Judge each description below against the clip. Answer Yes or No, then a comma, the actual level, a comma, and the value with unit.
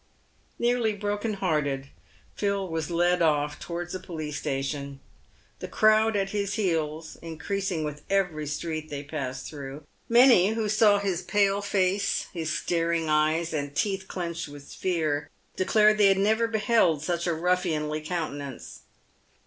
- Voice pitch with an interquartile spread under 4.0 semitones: No, average, 4.6 semitones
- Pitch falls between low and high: Yes, medium, 170 Hz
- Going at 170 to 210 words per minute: No, average, 140 wpm